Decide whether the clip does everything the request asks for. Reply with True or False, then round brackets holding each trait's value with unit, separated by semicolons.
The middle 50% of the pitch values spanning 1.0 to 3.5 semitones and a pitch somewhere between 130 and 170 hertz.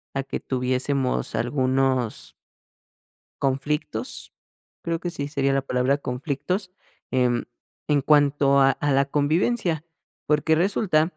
True (2.7 semitones; 140 Hz)